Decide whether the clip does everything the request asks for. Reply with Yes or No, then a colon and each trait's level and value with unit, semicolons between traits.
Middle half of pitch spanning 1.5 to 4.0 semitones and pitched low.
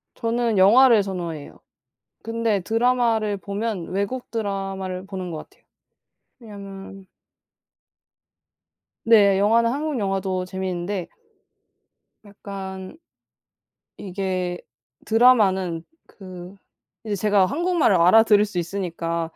No: average, 3.2 semitones; high, 195 Hz